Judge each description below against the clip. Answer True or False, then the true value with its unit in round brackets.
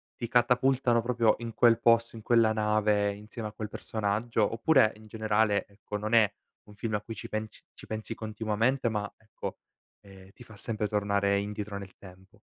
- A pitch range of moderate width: False (1.9 semitones)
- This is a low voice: True (110 Hz)